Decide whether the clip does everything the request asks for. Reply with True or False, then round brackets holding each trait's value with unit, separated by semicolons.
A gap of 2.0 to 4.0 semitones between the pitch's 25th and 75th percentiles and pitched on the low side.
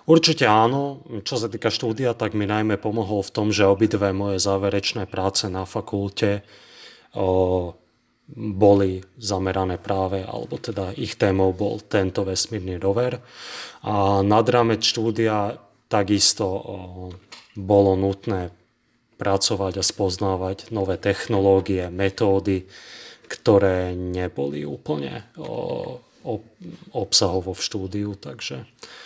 True (2.4 semitones; 100 Hz)